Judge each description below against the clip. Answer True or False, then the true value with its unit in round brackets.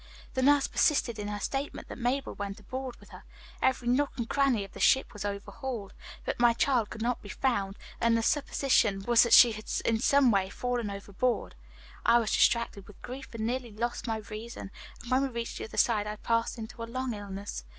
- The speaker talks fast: True (215 wpm)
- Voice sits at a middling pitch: False (235 Hz)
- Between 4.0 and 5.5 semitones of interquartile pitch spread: False (3.5 semitones)